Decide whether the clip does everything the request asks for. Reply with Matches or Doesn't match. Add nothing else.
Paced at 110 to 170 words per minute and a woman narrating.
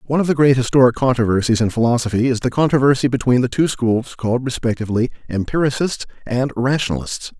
Doesn't match